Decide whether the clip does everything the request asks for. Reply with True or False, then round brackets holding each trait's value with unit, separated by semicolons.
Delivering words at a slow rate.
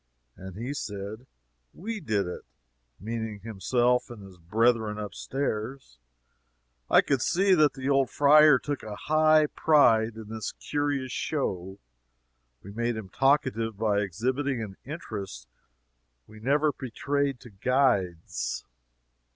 True (125 wpm)